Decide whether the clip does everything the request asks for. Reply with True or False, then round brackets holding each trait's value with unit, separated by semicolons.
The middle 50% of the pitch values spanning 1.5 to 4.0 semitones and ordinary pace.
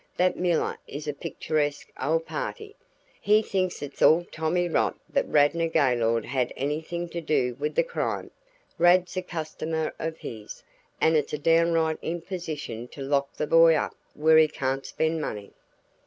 True (2.9 semitones; 160 wpm)